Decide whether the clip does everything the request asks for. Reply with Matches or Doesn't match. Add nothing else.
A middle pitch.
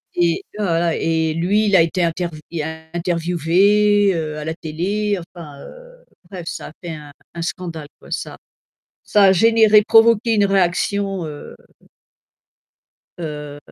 Matches